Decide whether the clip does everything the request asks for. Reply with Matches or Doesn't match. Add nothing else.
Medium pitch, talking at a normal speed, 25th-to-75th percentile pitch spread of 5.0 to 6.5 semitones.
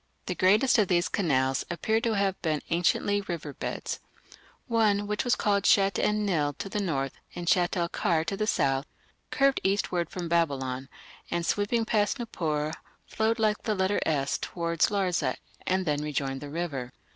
Matches